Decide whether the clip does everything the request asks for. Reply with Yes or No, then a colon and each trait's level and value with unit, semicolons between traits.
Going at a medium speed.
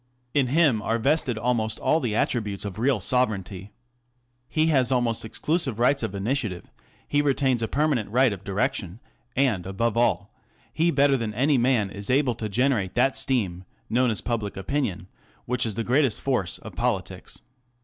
Yes: average, 170 wpm